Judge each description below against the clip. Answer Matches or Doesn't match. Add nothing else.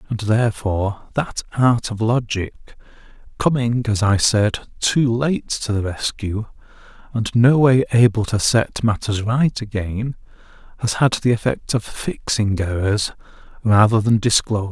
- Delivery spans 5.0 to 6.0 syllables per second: Doesn't match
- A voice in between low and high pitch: Doesn't match